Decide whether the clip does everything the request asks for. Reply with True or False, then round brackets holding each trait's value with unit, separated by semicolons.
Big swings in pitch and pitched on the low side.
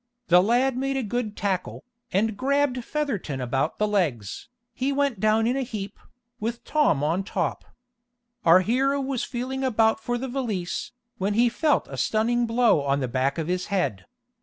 False (5.9 semitones; 225 Hz)